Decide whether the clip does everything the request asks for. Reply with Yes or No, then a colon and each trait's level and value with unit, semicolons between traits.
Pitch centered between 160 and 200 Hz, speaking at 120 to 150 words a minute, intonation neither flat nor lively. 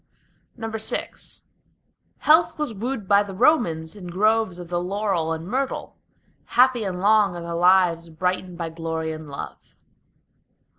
Yes: medium, 185 Hz; average, 140 wpm; average, 4.5 semitones